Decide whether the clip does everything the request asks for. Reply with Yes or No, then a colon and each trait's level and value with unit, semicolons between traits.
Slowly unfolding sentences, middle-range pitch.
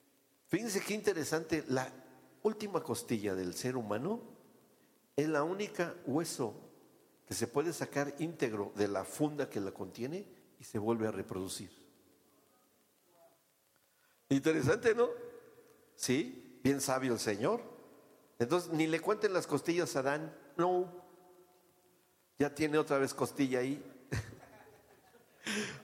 Yes: slow, 120 wpm; medium, 145 Hz